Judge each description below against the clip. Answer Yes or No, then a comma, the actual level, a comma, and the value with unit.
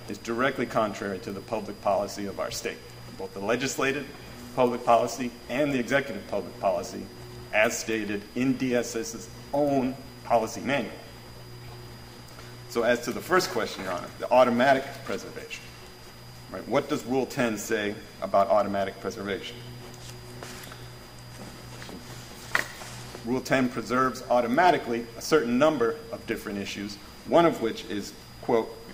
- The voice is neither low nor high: No, low, 120 Hz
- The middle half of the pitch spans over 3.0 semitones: No, average, 2.7 semitones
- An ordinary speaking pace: No, slow, 130 wpm